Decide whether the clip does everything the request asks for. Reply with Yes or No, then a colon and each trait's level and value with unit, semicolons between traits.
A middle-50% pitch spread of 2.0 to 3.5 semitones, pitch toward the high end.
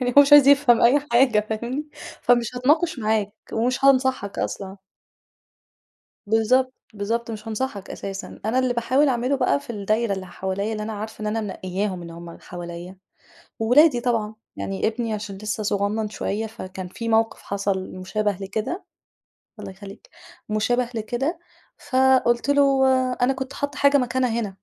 No: average, 4.1 semitones; high, 225 Hz